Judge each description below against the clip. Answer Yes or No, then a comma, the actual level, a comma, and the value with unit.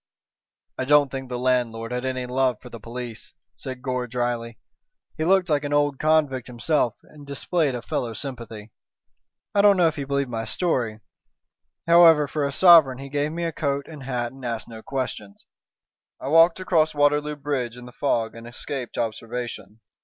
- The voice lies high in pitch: No, low, 130 Hz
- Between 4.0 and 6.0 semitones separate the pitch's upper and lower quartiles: No, average, 3.5 semitones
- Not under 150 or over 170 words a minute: No, average, 180 wpm